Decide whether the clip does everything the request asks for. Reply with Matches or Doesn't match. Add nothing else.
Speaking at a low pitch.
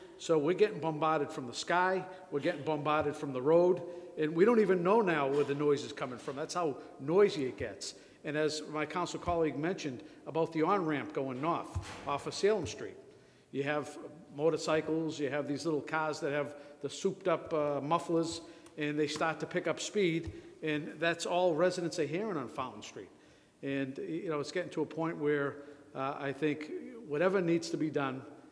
Doesn't match